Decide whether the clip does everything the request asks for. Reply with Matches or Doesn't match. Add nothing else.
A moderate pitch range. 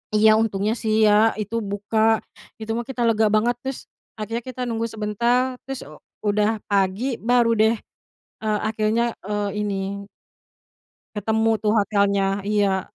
Doesn't match